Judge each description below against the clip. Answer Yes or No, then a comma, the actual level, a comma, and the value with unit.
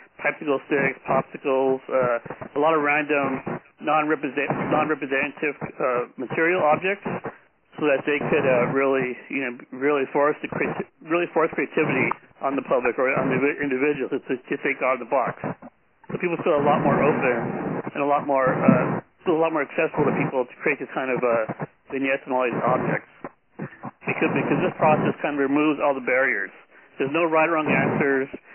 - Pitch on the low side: No, medium, 145 Hz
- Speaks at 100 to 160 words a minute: No, average, 185 wpm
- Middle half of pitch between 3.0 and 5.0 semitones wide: No, narrow, 2.4 semitones